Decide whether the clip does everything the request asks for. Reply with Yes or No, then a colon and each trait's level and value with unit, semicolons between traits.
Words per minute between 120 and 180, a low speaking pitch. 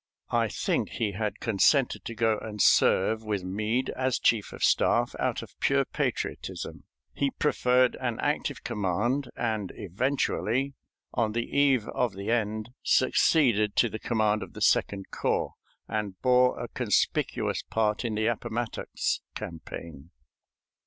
Yes: average, 140 wpm; low, 110 Hz